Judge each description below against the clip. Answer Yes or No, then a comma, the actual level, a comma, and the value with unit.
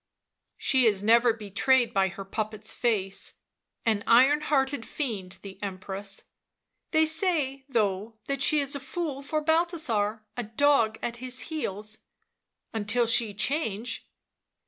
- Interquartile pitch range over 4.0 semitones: Yes, average, 5.1 semitones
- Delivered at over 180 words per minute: No, average, 145 wpm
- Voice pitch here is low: No, high, 230 Hz